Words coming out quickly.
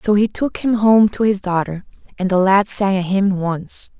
Yes: fast, 225 wpm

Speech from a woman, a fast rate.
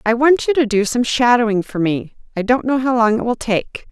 Yes: female; fast, 260 wpm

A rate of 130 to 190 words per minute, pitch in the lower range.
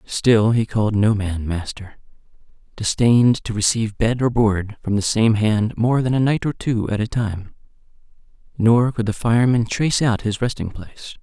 Yes: average, 180 wpm; low, 110 Hz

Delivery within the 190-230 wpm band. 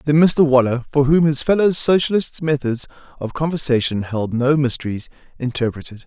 No: average, 150 wpm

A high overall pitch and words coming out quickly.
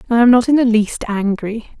Yes: high, 230 Hz; fast, 235 wpm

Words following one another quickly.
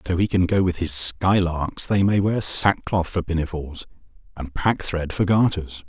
No: average, 175 wpm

